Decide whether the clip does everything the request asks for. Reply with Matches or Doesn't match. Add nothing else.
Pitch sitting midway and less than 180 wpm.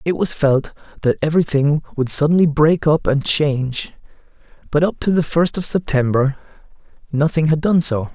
Matches